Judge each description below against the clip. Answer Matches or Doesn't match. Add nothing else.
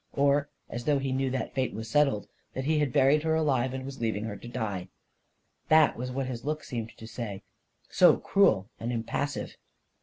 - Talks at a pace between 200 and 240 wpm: Matches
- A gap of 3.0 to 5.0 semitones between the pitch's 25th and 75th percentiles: Matches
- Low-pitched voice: Matches